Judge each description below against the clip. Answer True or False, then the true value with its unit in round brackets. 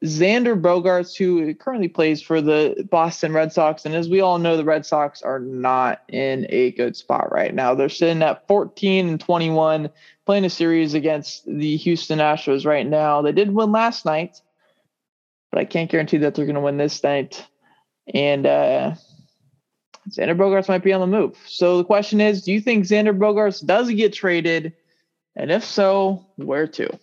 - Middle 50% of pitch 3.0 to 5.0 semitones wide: True (4.0 semitones)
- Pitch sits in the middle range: True (165 Hz)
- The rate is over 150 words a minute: True (185 wpm)